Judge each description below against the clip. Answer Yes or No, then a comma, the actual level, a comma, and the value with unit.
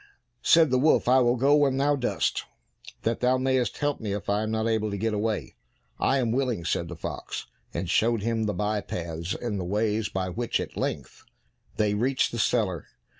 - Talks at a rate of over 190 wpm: Yes, average, 200 wpm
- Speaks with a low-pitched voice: Yes, low, 110 Hz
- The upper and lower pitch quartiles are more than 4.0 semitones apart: No, average, 3.7 semitones